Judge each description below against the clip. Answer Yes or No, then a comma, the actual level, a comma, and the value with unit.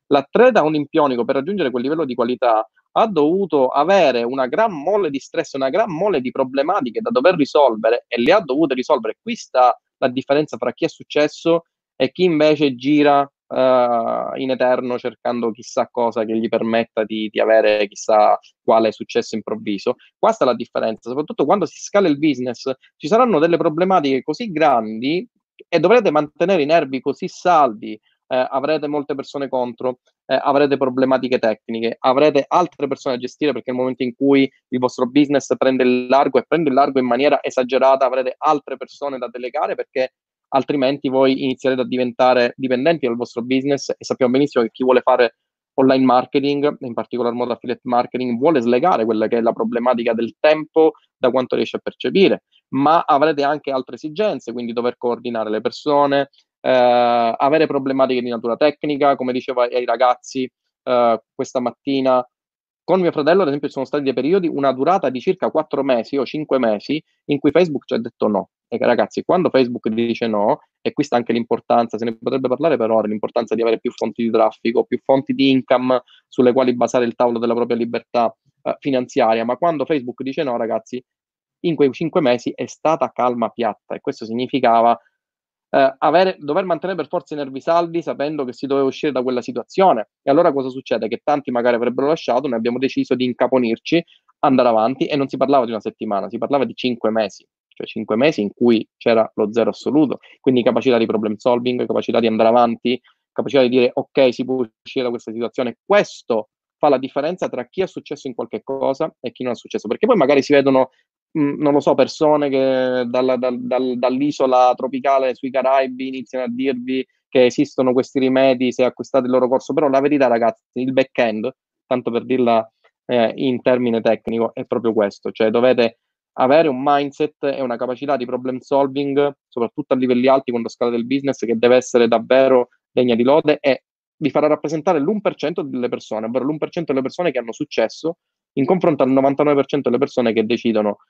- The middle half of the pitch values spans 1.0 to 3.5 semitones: Yes, average, 2.9 semitones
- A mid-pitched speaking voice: No, low, 130 Hz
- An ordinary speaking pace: No, fast, 190 wpm